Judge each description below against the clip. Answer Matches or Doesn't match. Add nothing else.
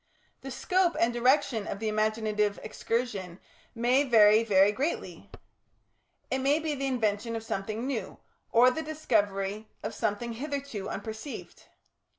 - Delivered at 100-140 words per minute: Matches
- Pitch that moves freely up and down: Doesn't match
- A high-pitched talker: Matches